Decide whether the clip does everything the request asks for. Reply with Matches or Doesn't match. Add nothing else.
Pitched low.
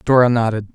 Matches